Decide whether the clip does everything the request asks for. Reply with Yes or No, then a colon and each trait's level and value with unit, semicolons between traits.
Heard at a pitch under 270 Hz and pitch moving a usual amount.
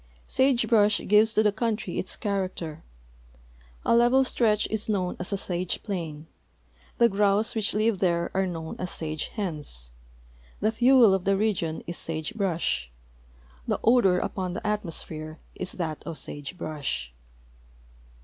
Yes: high, 190 Hz; average, 4.6 semitones